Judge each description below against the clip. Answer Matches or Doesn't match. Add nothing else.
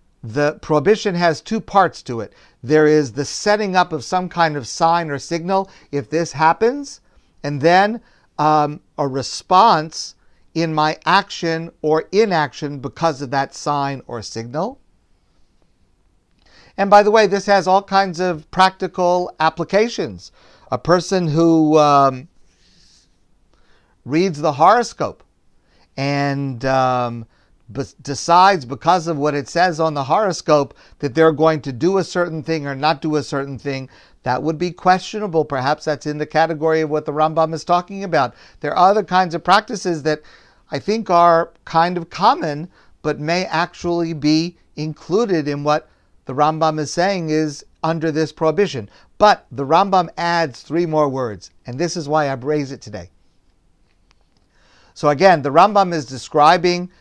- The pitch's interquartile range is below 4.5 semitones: Matches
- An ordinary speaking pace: Matches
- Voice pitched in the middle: Matches